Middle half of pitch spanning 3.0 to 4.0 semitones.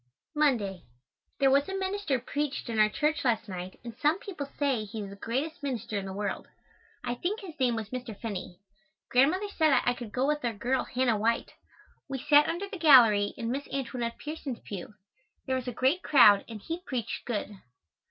No: average, 5.1 semitones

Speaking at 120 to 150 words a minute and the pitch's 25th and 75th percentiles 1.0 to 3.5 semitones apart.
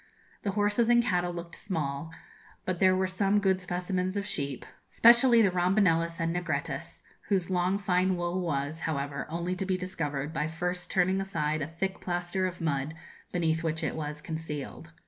No: average, 170 wpm; average, 2.8 semitones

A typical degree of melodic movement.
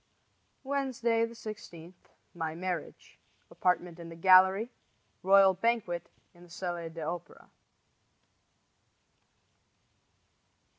Yes: average, 4.3 semitones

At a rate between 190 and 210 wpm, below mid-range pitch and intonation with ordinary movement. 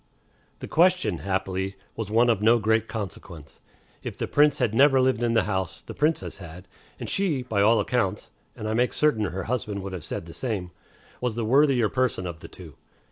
Yes: average, 200 wpm; low, 110 Hz; average, 4.7 semitones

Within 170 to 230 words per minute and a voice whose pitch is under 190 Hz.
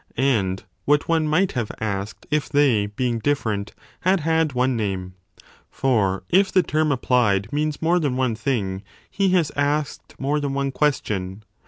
No: average, 160 wpm; low, 135 Hz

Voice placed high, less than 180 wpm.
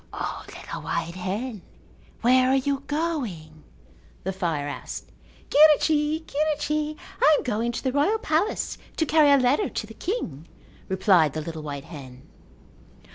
Yes: very high, 255 Hz; average, 145 wpm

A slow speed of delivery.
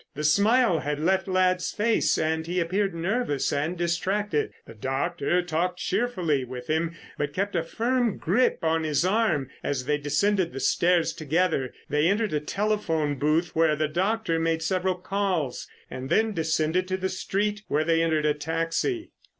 No: average, 165 wpm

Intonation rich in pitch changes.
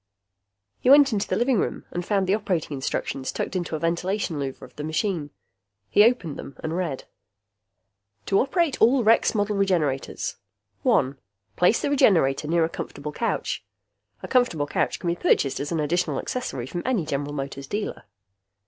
Yes: wide, 6.4 semitones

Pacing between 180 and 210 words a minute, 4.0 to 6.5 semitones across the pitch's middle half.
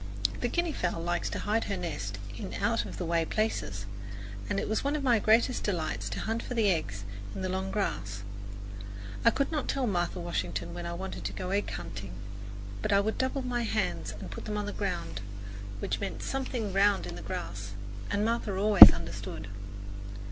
Yes: average, 200 wpm; average, 5.1 semitones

